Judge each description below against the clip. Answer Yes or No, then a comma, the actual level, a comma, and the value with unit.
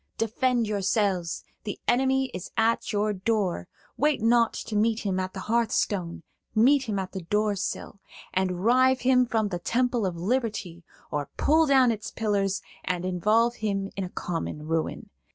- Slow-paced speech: No, average, 160 wpm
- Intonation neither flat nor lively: Yes, average, 4.1 semitones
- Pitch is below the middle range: No, high, 210 Hz